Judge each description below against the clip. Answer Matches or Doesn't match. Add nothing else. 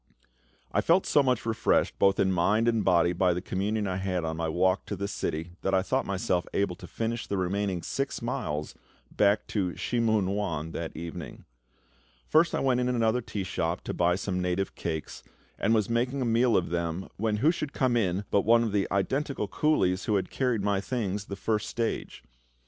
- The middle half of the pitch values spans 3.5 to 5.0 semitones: Matches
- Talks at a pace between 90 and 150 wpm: Doesn't match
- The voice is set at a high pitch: Doesn't match